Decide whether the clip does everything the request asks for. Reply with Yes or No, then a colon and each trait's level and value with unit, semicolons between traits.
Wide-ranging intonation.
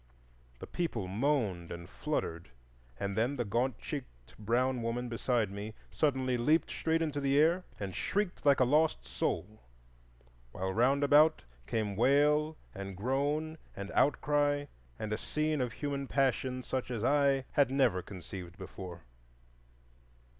Yes: wide, 5.8 semitones